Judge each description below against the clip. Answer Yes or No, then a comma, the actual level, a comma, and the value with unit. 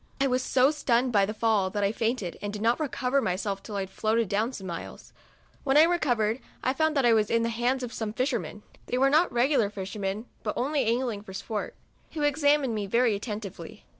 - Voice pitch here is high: Yes, high, 230 Hz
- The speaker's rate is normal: No, fast, 220 wpm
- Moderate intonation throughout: Yes, average, 4.2 semitones